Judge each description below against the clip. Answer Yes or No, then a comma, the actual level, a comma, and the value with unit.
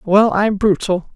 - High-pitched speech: Yes, high, 200 Hz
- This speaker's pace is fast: No, average, 155 wpm